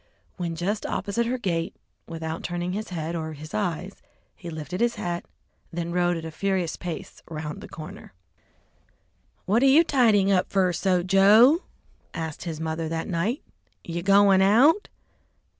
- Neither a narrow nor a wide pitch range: Yes, average, 3.6 semitones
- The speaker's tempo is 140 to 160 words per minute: Yes, average, 155 wpm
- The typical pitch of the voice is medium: Yes, medium, 180 Hz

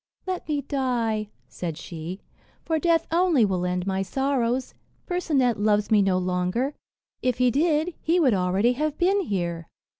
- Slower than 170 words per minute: Yes, average, 155 wpm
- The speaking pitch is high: Yes, high, 245 Hz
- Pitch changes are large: Yes, wide, 8.1 semitones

